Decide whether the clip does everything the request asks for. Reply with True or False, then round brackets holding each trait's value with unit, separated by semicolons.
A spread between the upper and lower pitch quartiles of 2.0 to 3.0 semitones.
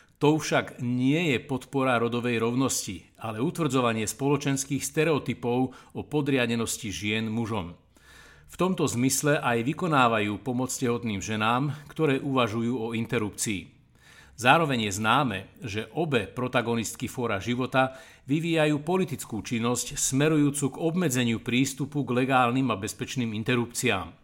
False (3.6 semitones)